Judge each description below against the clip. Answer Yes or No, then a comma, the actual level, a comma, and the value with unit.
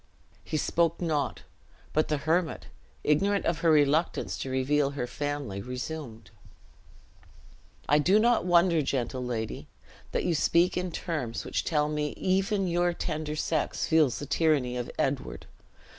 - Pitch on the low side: No, medium, 150 Hz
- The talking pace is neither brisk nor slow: Yes, average, 145 wpm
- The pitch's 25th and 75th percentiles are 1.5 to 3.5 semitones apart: No, average, 4.0 semitones